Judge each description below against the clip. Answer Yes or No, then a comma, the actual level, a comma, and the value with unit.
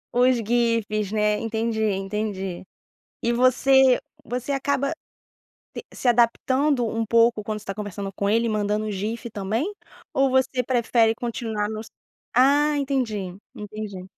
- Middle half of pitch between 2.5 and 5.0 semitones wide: Yes, average, 3.2 semitones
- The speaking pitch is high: Yes, high, 225 Hz